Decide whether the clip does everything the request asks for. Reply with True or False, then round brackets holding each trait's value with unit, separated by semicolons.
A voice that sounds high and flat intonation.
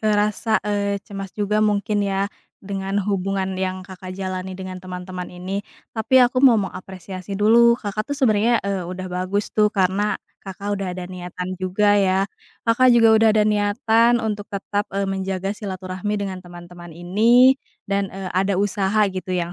True (195 Hz; 2.1 semitones)